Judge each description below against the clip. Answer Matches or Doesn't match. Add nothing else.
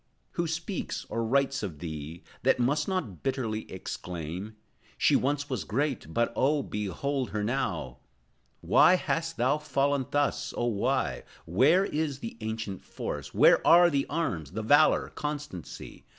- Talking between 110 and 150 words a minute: Matches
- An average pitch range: Doesn't match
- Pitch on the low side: Matches